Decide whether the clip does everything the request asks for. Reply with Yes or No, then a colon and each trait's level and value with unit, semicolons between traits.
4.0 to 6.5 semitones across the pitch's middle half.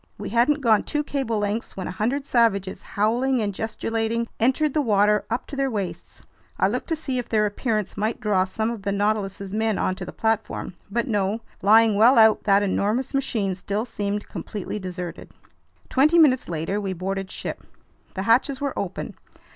No: average, 3.2 semitones